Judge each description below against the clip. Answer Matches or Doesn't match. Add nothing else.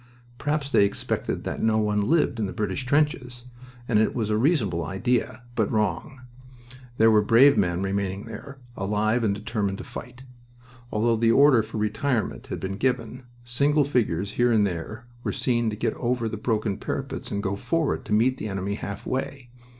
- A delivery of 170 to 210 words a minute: Matches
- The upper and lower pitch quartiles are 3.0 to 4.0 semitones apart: Matches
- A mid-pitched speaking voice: Doesn't match